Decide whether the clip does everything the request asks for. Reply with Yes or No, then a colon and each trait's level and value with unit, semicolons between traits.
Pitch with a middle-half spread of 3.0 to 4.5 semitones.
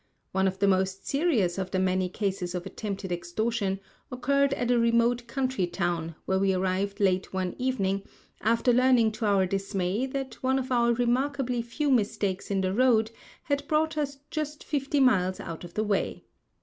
No: average, 5.3 semitones